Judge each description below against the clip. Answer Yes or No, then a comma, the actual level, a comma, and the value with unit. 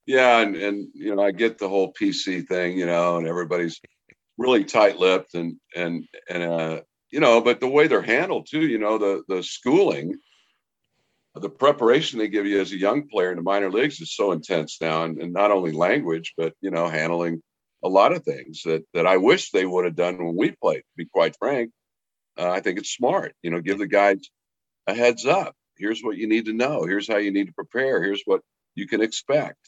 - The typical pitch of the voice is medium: No, very low, 95 Hz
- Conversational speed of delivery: No, fast, 220 wpm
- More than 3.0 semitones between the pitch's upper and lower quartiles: Yes, average, 4.0 semitones